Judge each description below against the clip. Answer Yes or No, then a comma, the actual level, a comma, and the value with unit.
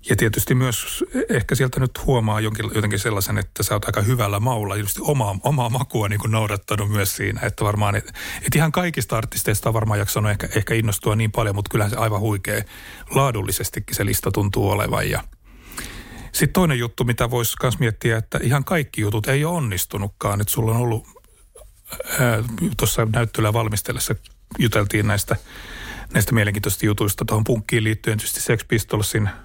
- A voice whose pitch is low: Yes, low, 110 Hz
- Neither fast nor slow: No, fast, 165 wpm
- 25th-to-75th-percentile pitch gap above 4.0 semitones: No, average, 2.7 semitones